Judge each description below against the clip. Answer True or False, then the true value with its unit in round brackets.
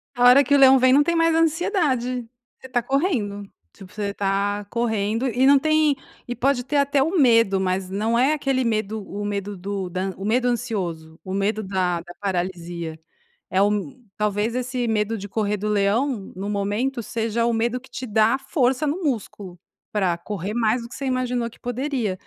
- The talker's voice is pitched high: True (225 Hz)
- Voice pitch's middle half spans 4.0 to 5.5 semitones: True (4.6 semitones)